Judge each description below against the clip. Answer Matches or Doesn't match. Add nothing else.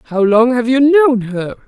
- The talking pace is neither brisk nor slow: Doesn't match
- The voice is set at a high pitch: Matches